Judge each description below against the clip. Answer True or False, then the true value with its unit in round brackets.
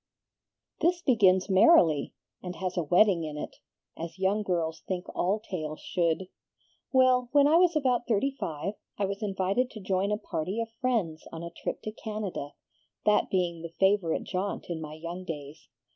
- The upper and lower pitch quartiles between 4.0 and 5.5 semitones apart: True (4.4 semitones)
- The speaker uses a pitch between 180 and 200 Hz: True (190 Hz)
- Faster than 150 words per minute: True (175 wpm)